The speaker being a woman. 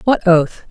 Yes: female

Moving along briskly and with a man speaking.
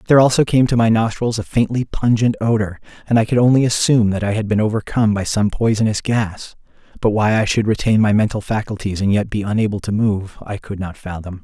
Yes: fast, 220 wpm; male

